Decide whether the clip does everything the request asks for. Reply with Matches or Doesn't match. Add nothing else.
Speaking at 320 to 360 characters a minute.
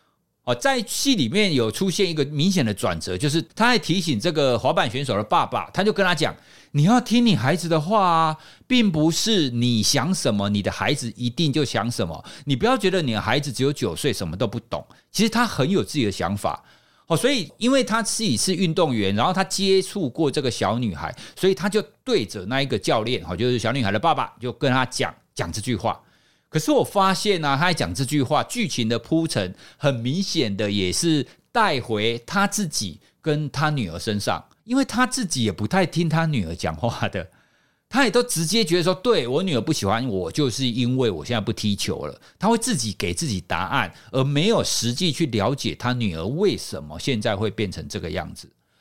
Doesn't match